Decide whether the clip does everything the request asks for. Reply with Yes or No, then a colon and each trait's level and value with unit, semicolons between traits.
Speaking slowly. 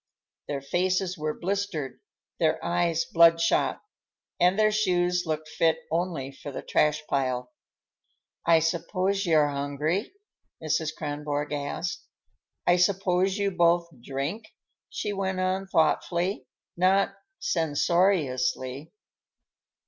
Yes: slow, 110 wpm